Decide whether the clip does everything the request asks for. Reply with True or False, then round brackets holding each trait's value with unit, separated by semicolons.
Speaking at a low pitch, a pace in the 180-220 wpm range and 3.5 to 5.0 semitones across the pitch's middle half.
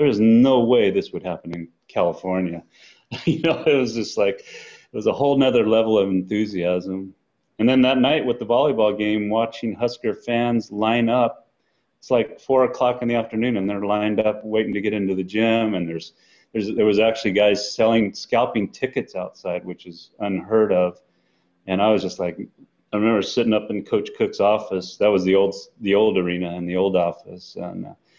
True (105 Hz; 200 wpm; 4.0 semitones)